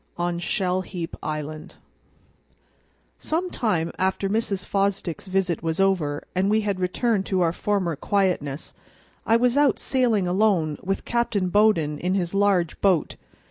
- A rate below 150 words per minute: Yes, average, 140 wpm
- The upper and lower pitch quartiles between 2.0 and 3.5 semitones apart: Yes, average, 3.2 semitones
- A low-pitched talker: No, high, 190 Hz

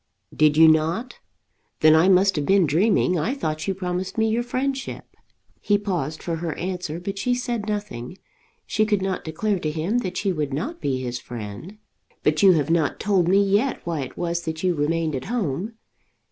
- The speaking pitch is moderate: Yes, medium, 180 Hz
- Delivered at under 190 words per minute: No, average, 195 wpm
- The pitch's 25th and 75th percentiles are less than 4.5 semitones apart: No, average, 4.8 semitones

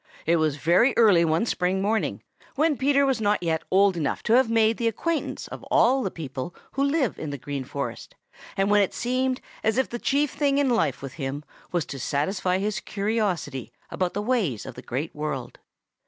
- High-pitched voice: Yes, high, 200 Hz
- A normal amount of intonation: No, wide, 7.7 semitones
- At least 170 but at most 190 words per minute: No, average, 200 wpm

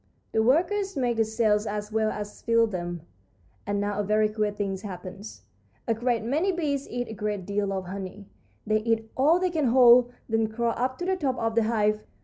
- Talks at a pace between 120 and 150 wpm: No, fast, 205 wpm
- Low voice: No, high, 220 Hz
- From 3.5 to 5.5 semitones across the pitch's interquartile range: No, average, 3.1 semitones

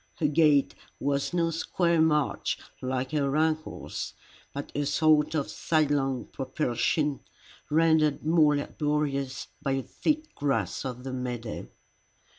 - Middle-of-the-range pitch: Yes, medium, 145 Hz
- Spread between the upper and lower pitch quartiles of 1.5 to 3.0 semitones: Yes, narrow, 2.5 semitones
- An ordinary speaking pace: No, slow, 120 wpm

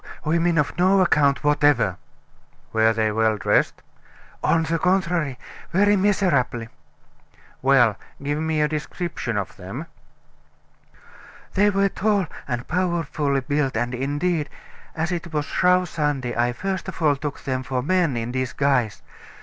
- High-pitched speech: No, medium, 150 Hz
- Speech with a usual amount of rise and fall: No, wide, 5.7 semitones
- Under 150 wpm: Yes, slow, 135 wpm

